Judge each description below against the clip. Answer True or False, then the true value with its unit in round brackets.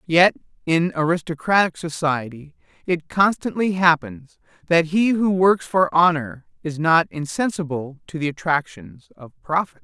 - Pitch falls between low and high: True (165 Hz)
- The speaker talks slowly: True (130 wpm)